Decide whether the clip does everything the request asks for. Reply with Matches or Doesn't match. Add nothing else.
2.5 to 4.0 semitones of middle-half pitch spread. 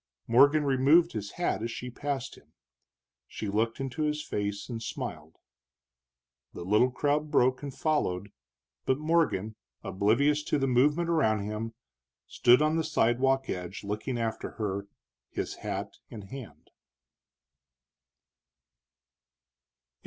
Doesn't match